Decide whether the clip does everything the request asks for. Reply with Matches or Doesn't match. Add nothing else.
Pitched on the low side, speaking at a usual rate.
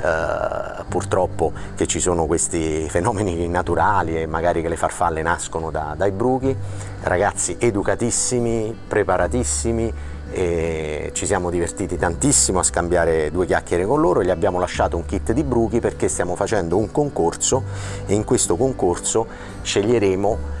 Matches